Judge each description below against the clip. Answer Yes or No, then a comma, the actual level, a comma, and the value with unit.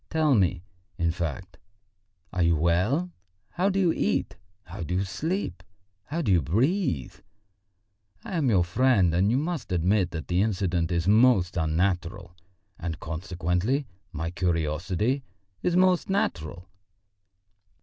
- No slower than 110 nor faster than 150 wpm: Yes, slow, 135 wpm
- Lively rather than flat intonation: Yes, wide, 7.5 semitones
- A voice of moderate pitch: No, very low, 90 Hz